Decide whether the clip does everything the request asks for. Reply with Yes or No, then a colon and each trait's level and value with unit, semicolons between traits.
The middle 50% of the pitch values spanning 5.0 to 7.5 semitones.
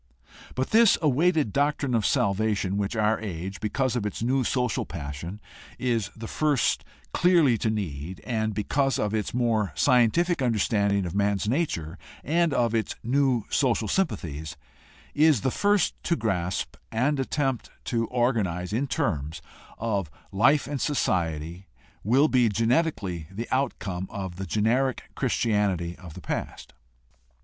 Yes: wide, 5.5 semitones